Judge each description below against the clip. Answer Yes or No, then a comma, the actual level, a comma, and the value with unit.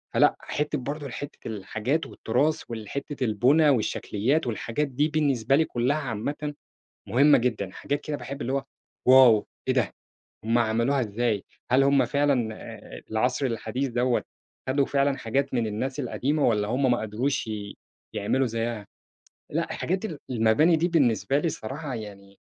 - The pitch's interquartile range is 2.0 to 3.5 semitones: No, average, 4.3 semitones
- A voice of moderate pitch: No, low, 130 Hz